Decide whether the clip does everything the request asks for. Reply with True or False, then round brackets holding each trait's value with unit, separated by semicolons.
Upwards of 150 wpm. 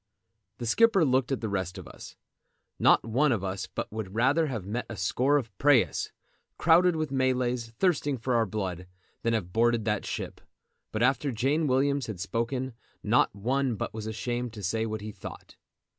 True (185 wpm)